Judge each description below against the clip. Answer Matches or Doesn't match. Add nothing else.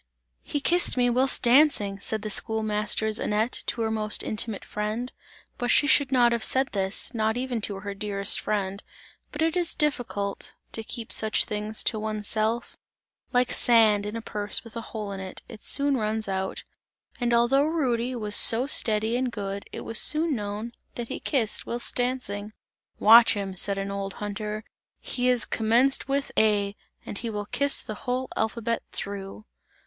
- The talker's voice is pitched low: Doesn't match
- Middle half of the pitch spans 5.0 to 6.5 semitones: Doesn't match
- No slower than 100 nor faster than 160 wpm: Doesn't match